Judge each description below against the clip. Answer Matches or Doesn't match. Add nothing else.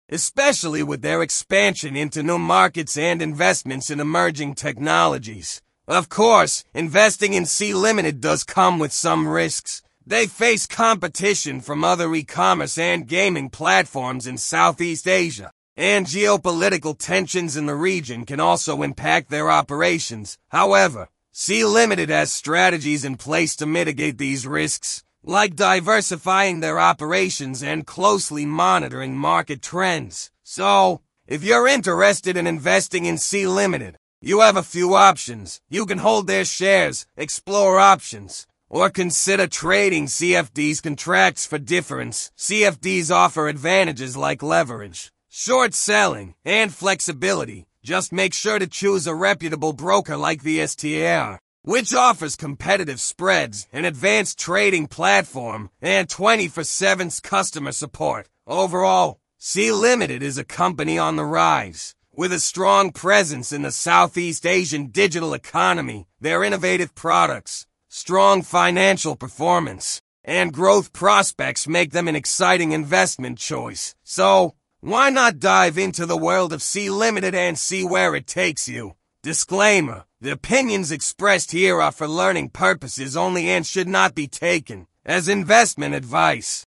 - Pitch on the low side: Doesn't match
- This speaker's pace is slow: Matches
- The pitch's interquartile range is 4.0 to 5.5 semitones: Matches